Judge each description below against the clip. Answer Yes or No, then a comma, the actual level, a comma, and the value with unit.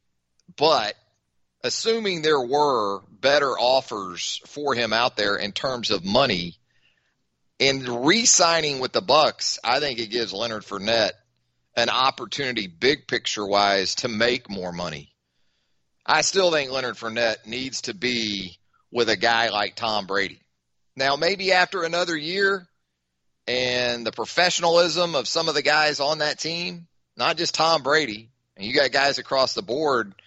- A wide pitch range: Yes, wide, 8.1 semitones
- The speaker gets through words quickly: No, average, 150 wpm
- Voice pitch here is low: Yes, low, 120 Hz